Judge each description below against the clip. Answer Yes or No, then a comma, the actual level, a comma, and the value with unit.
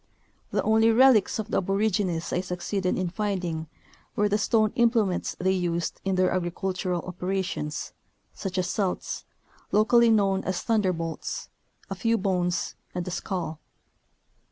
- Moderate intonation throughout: Yes, average, 3.0 semitones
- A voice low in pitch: No, high, 190 Hz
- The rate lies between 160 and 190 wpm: No, slow, 135 wpm